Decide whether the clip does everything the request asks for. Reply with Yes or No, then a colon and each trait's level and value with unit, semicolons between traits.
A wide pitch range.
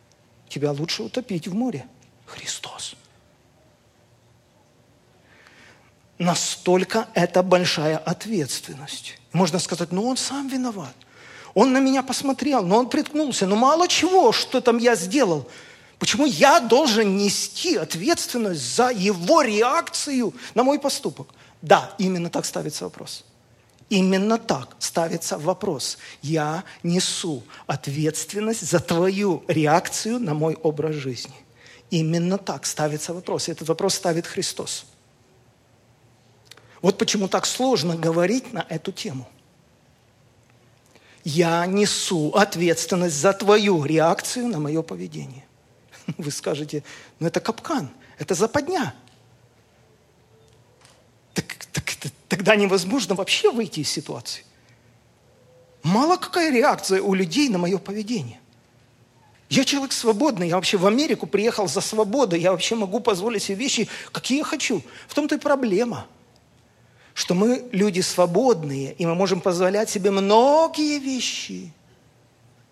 Yes: wide, 7.1 semitones